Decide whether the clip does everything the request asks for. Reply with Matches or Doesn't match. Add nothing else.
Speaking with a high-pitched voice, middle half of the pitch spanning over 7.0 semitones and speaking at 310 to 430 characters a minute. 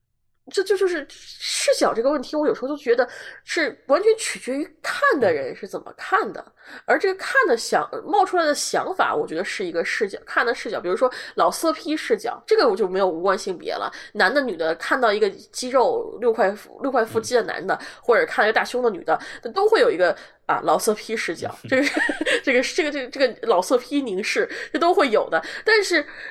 Matches